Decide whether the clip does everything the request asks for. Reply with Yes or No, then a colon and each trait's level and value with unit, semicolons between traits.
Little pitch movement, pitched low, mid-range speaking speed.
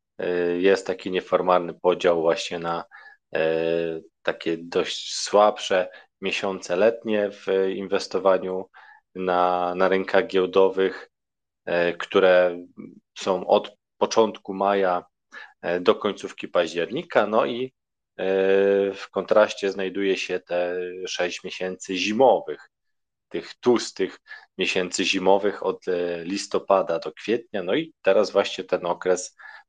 No: narrow, 1.6 semitones; very low, 95 Hz; slow, 100 wpm